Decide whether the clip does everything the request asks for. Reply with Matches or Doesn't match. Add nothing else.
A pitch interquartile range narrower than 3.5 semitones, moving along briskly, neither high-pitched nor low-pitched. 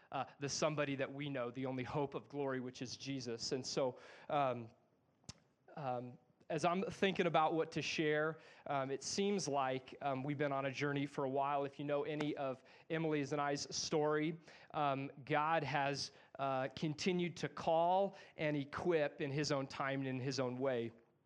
Doesn't match